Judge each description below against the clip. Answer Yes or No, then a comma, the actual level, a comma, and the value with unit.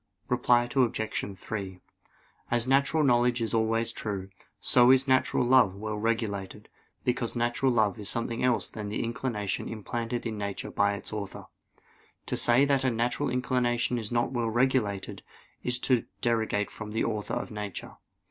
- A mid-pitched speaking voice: No, low, 115 Hz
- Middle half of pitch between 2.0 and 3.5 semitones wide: Yes, average, 2.7 semitones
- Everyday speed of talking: Yes, average, 155 wpm